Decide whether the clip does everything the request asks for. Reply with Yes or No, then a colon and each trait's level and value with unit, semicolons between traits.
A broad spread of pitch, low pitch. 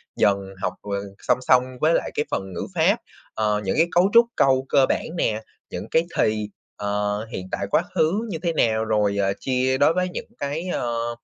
Yes: wide, 7.2 semitones; low, 125 Hz